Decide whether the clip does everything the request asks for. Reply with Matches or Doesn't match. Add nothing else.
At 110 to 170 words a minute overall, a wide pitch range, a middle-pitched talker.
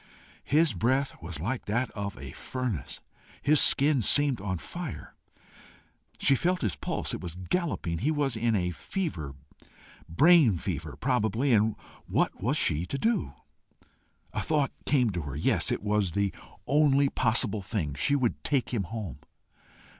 Doesn't match